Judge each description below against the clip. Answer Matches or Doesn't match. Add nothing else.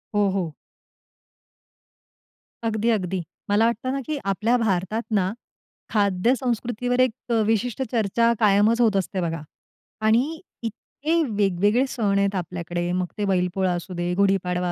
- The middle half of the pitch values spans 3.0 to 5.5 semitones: Matches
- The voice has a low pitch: Doesn't match